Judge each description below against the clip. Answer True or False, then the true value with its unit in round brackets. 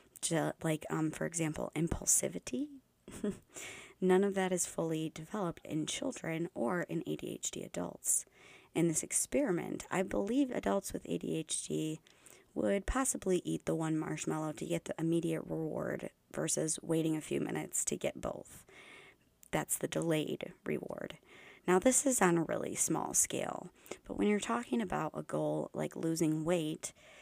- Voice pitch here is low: False (165 Hz)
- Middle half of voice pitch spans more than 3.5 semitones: False (3.1 semitones)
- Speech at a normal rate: True (145 wpm)